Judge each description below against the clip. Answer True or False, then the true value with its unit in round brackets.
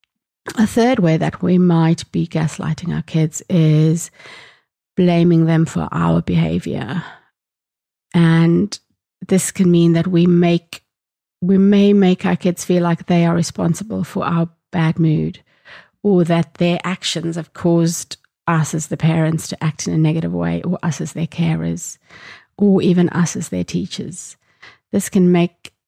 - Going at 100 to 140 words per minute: False (155 wpm)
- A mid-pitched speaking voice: True (170 Hz)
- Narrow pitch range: True (2.0 semitones)